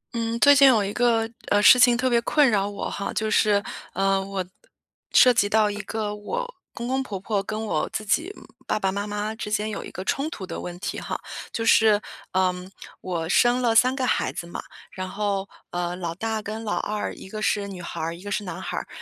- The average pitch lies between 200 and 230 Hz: Yes, high, 210 Hz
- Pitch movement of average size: Yes, average, 3.0 semitones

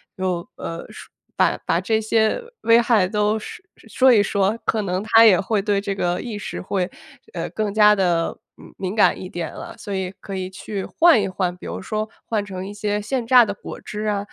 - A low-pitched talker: No, high, 205 Hz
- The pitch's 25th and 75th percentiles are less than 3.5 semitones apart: Yes, average, 2.7 semitones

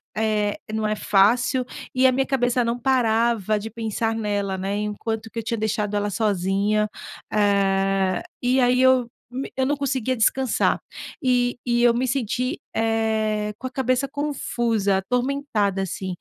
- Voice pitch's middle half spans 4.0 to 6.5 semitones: No, average, 3.3 semitones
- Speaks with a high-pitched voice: Yes, high, 225 Hz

